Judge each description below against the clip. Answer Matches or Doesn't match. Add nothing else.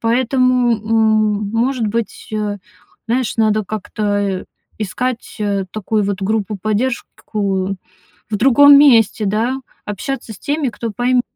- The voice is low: Doesn't match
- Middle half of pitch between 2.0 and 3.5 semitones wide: Matches